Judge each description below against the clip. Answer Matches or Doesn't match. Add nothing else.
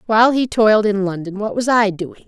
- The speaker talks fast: Matches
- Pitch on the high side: Matches